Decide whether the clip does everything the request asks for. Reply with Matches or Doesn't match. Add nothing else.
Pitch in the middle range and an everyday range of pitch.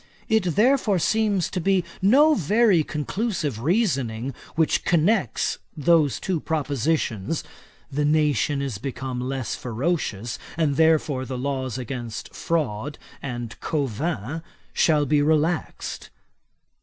Matches